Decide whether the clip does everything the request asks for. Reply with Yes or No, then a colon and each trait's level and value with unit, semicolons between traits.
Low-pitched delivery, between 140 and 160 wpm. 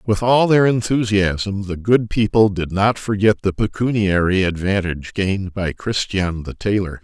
Yes: low, 100 Hz; average, 155 wpm